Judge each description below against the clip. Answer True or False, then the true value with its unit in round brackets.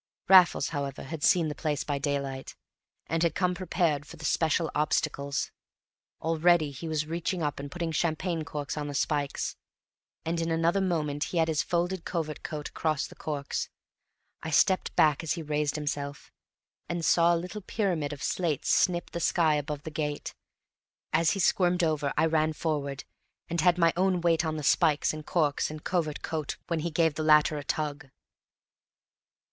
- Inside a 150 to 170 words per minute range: False (180 wpm)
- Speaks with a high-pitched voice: False (155 Hz)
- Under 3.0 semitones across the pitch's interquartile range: True (2.5 semitones)